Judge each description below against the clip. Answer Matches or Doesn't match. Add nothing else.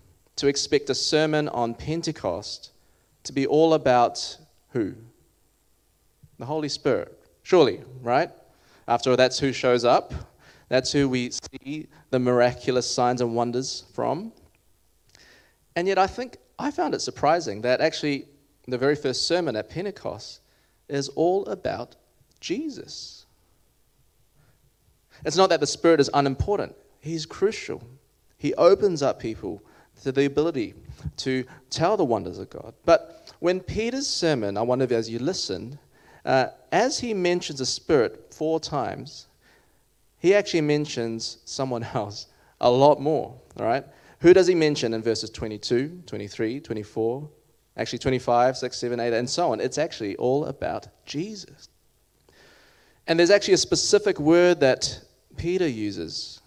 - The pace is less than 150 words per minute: Matches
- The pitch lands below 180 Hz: Matches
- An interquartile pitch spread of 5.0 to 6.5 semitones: Matches